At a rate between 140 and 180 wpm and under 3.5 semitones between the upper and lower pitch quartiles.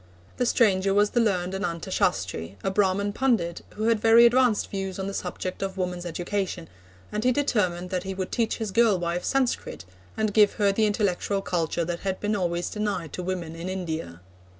No: average, 195 wpm; average, 3.1 semitones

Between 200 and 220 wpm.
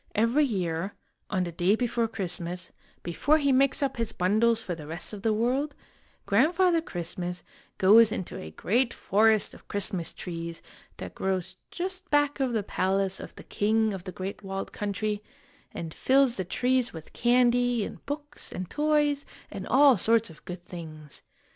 No: average, 165 wpm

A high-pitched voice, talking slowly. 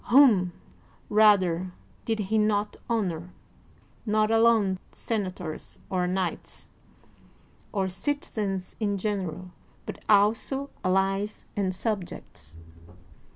Yes: high, 200 Hz; slow, 95 wpm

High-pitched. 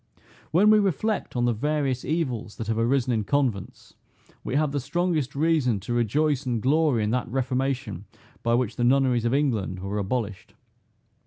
No: low, 130 Hz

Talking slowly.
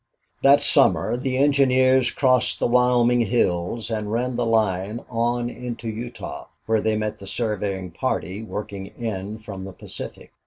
No: average, 155 wpm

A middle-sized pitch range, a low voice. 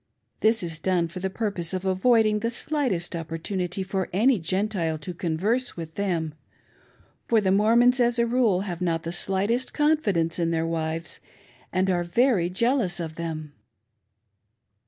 No: average, 5.0 semitones; medium, 185 Hz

